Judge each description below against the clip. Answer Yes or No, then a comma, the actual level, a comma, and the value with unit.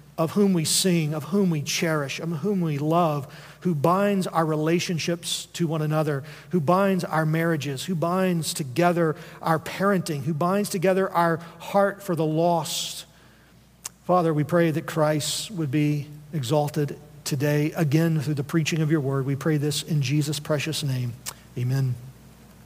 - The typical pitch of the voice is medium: Yes, medium, 160 Hz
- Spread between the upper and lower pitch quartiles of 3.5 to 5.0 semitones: No, narrow, 2.5 semitones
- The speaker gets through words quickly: No, average, 160 wpm